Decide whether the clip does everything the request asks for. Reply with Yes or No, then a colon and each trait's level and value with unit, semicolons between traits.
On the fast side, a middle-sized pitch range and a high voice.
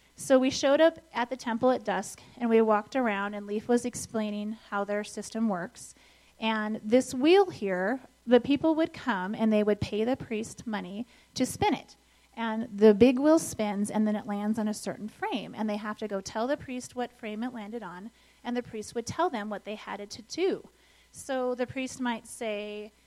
Yes: fast, 215 wpm; average, 3.0 semitones; high, 225 Hz